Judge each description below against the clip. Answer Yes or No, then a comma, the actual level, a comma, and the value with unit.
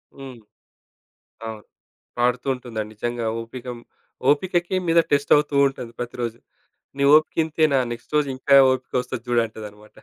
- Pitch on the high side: No, low, 125 Hz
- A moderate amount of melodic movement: Yes, average, 3.5 semitones